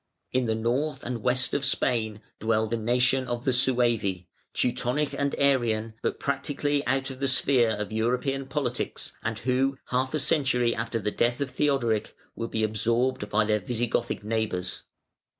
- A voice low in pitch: Yes, low, 120 Hz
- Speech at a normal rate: Yes, average, 165 wpm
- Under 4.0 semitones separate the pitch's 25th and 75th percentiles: Yes, average, 3.2 semitones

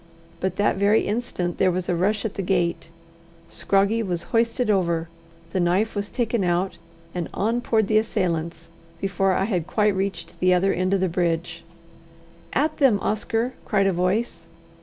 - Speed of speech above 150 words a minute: Yes, average, 170 wpm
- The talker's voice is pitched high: Yes, high, 195 Hz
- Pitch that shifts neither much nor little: Yes, average, 3.4 semitones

